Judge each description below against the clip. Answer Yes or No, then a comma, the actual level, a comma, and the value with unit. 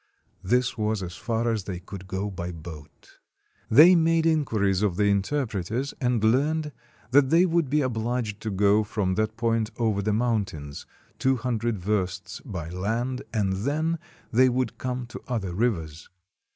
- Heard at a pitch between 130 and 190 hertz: No, low, 110 Hz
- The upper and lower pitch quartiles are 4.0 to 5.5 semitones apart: Yes, average, 4.7 semitones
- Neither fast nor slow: Yes, average, 160 wpm